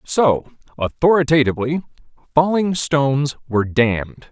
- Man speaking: Yes, male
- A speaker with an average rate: No, slow, 85 wpm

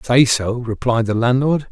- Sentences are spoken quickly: No, average, 175 wpm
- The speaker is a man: Yes, male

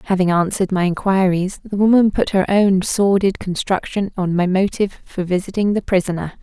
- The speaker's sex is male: No, female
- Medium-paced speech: Yes, average, 170 wpm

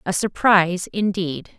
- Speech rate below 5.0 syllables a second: Yes, 4.4 syllables/s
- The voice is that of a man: No, female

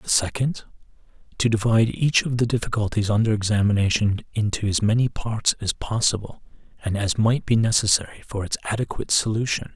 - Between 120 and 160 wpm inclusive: Yes, average, 155 wpm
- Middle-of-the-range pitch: No, low, 110 Hz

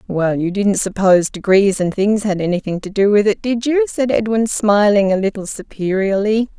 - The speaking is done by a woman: Yes, female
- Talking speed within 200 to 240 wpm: No, average, 190 wpm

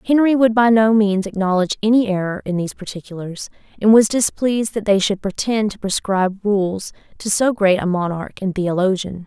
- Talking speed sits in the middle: Yes, average, 180 wpm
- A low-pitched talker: No, high, 205 Hz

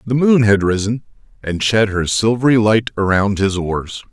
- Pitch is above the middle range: No, low, 110 Hz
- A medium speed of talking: Yes, average, 175 wpm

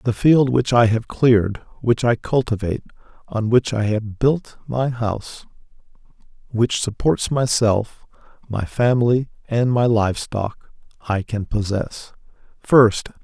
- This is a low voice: Yes, low, 115 Hz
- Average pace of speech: No, slow, 125 wpm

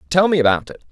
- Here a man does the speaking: Yes, male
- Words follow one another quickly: Yes, fast, 265 wpm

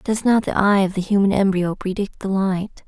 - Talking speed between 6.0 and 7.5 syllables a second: No, 5.0 syllables/s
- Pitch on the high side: Yes, high, 195 Hz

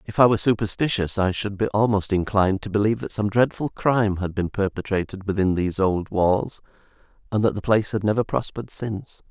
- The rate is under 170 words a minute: No, average, 195 wpm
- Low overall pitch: Yes, low, 100 Hz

